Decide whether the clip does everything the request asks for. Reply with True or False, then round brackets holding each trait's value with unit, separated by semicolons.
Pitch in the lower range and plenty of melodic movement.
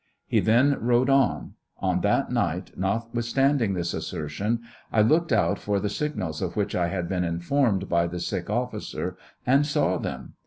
True (105 Hz; 6.0 semitones)